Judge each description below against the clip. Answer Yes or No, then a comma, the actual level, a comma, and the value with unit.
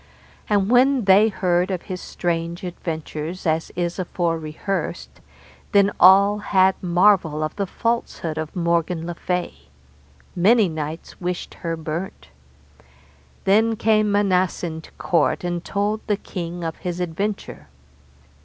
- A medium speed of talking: No, slow, 130 wpm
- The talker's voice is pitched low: No, medium, 180 Hz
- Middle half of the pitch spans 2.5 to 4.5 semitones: Yes, average, 3.2 semitones